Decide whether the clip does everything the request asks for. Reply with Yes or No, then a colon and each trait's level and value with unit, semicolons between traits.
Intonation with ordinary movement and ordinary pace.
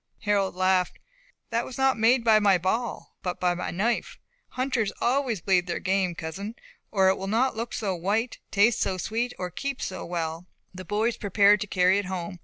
Yes: average, 3.8 semitones; average, 195 wpm